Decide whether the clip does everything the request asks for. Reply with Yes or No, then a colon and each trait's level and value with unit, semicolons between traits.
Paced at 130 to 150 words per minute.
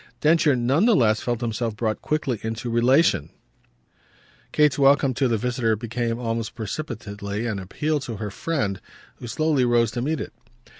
No: average, 160 wpm